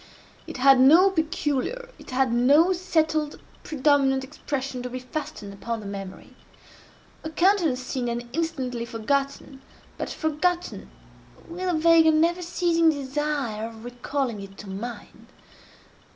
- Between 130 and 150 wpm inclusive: Yes, slow, 135 wpm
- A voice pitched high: Yes, very high, 275 Hz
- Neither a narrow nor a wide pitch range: Yes, average, 4.9 semitones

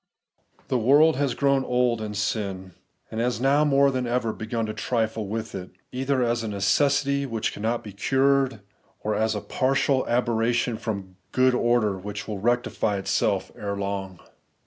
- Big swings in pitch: No, average, 3.8 semitones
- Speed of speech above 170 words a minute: No, average, 165 wpm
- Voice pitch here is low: Yes, low, 115 Hz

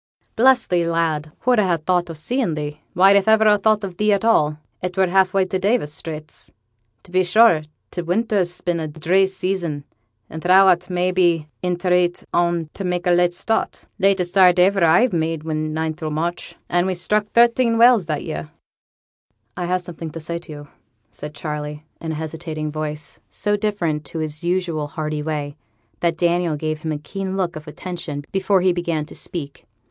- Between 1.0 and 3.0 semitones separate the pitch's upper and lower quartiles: No, average, 3.4 semitones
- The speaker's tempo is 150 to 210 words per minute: Yes, average, 200 wpm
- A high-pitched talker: No, medium, 175 Hz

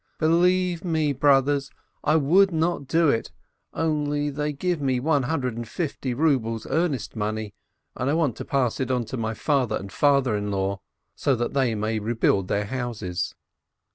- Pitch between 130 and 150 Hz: Yes, low, 135 Hz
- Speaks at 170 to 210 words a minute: Yes, average, 175 wpm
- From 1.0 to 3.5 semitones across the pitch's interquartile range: No, average, 5.3 semitones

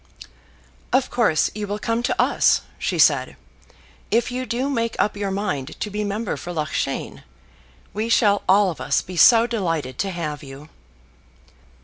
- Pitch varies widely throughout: Yes, wide, 5.7 semitones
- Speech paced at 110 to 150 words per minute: No, average, 160 wpm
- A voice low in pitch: No, high, 205 Hz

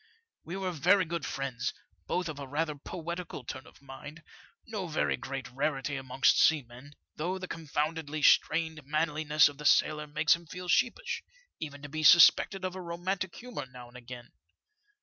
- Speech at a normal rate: Yes, average, 170 wpm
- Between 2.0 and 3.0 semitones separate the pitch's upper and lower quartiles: No, average, 3.6 semitones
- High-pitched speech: No, medium, 155 Hz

